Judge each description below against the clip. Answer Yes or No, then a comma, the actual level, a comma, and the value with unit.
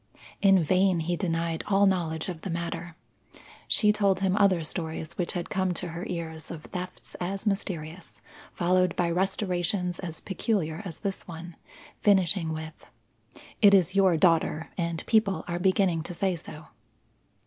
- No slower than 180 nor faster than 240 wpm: No, average, 155 wpm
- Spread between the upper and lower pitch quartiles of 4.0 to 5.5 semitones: No, narrow, 2.6 semitones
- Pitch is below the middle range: No, medium, 180 Hz